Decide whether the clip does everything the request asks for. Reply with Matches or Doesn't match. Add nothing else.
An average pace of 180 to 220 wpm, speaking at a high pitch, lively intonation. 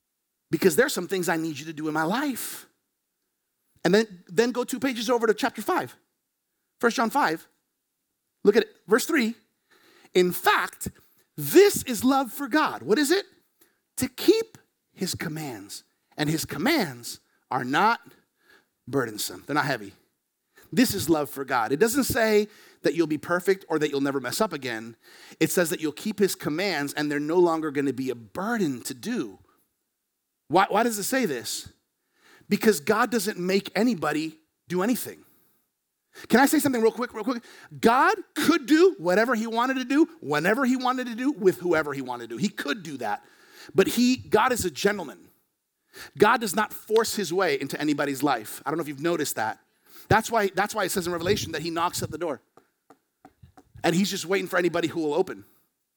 Matches